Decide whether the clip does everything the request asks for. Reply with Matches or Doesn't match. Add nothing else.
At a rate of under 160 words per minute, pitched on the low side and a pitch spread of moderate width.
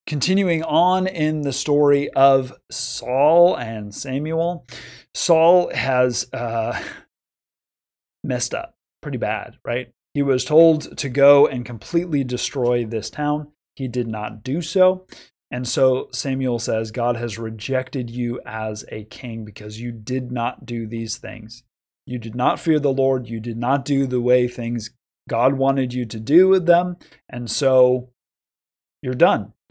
Matches